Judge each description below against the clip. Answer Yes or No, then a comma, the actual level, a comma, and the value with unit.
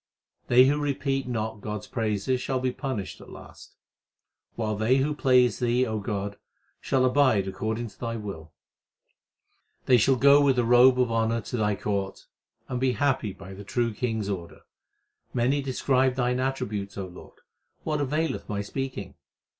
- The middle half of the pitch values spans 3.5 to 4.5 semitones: Yes, average, 4.0 semitones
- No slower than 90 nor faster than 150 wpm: No, average, 170 wpm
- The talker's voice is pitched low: Yes, low, 120 Hz